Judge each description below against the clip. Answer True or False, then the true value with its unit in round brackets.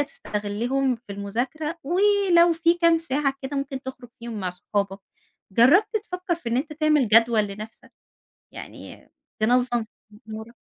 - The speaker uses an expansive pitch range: True (6.5 semitones)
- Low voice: False (260 Hz)